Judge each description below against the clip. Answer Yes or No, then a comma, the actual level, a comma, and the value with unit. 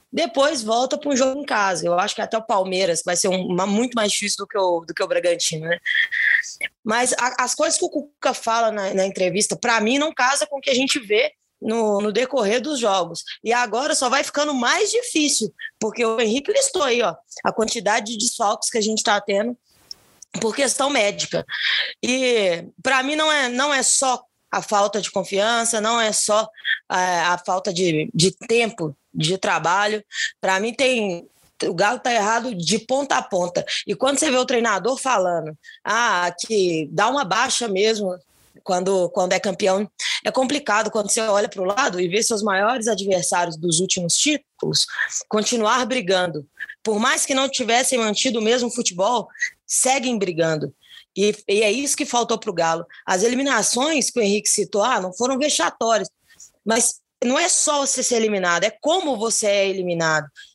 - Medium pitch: No, high, 220 Hz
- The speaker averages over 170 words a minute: Yes, fast, 185 wpm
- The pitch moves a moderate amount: Yes, average, 5.0 semitones